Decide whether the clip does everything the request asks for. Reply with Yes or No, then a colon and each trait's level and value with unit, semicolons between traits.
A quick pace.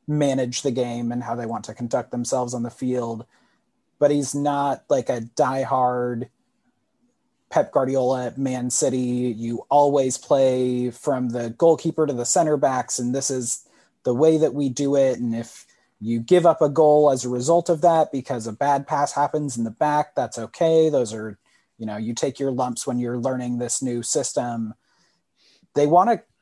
No: average, 185 wpm